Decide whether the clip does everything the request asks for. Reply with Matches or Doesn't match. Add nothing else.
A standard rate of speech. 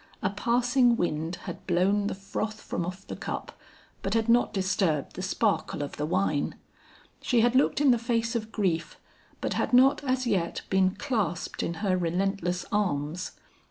Matches